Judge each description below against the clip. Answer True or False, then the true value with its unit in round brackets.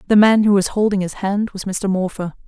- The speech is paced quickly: True (245 wpm)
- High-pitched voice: True (195 Hz)